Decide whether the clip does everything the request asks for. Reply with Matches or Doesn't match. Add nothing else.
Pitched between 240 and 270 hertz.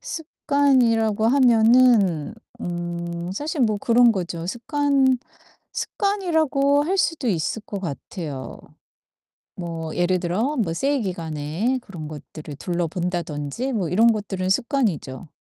Doesn't match